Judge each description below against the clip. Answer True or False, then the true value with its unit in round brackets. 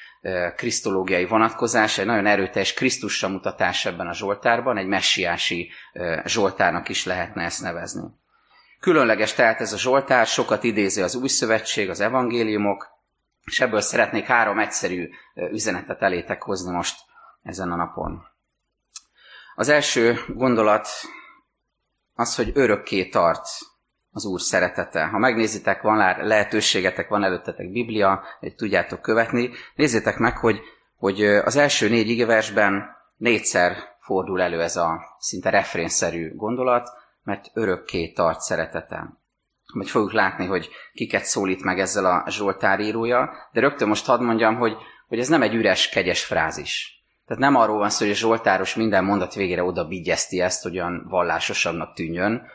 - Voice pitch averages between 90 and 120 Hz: True (105 Hz)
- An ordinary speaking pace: True (140 wpm)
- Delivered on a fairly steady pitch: False (3.6 semitones)